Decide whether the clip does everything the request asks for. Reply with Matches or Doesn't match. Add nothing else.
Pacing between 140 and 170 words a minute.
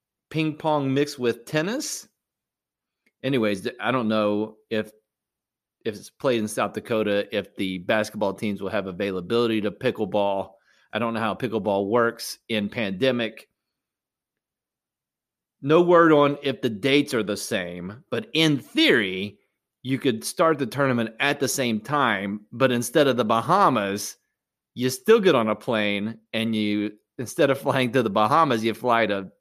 Matches